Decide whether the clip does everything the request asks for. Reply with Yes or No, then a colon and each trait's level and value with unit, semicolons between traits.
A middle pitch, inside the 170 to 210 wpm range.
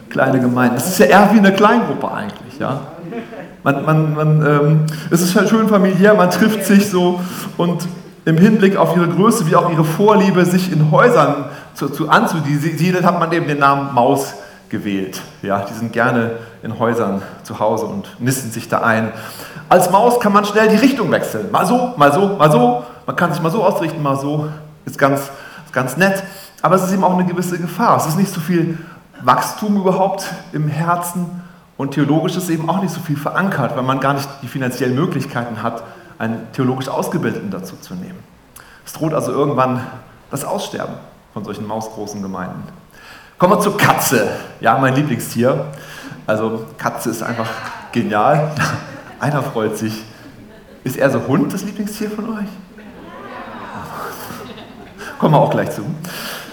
Yes: medium, 155 Hz; average, 175 wpm